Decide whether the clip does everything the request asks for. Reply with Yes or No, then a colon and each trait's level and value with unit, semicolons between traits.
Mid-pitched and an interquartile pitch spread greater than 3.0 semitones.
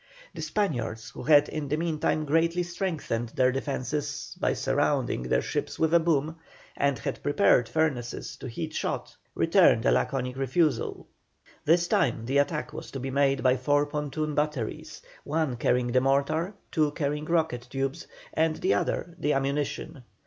Yes: medium, 145 Hz; average, 3.6 semitones